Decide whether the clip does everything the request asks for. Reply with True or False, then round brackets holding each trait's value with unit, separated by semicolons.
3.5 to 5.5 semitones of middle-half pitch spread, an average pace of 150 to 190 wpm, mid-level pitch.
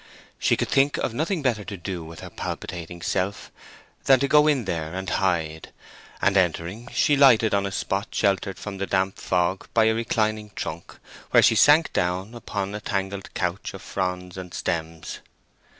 False (3.8 semitones; 180 wpm; 95 Hz)